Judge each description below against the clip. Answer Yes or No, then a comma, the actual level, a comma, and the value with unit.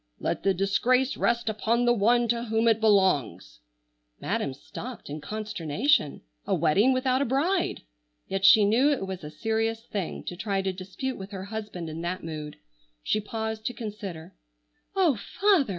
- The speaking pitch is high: Yes, high, 215 Hz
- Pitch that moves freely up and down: No, average, 4.2 semitones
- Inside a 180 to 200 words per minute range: No, average, 165 wpm